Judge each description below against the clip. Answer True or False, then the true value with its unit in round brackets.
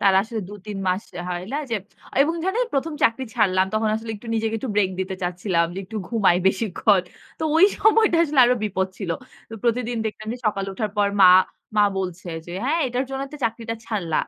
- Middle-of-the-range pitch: False (215 Hz)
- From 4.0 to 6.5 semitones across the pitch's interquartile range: True (4.4 semitones)